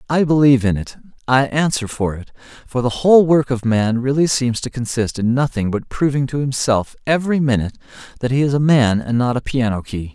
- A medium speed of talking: No, fast, 215 wpm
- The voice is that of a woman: No, male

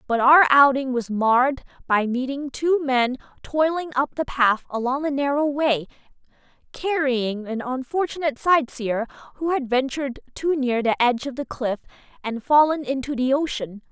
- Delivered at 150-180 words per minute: Yes, average, 155 wpm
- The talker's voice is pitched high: Yes, very high, 265 Hz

